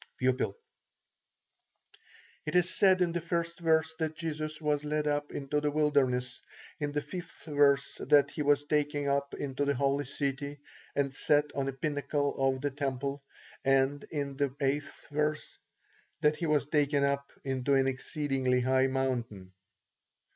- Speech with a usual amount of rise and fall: No, narrow, 1.8 semitones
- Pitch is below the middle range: No, medium, 145 Hz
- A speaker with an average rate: Yes, average, 155 wpm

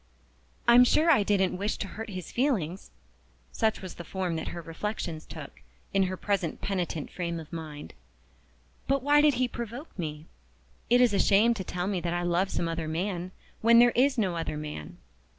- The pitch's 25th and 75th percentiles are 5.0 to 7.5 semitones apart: Yes, wide, 5.5 semitones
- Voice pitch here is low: No, high, 190 Hz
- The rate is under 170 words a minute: No, average, 190 wpm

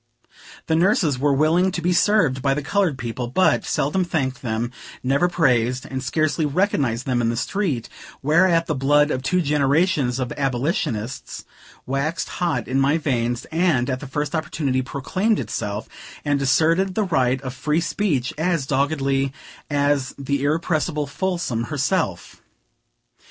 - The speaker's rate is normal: Yes, average, 150 wpm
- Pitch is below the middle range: No, medium, 145 Hz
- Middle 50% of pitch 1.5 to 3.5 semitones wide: No, average, 4.3 semitones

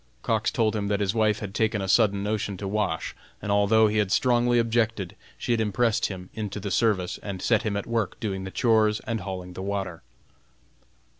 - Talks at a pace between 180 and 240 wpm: Yes, fast, 205 wpm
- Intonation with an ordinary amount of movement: No, narrow, 2.3 semitones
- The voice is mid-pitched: No, low, 105 Hz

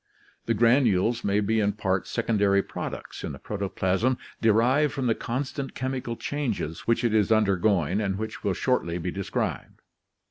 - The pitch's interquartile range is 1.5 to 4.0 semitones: Yes, average, 3.5 semitones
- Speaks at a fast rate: No, average, 155 wpm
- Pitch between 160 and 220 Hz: No, low, 110 Hz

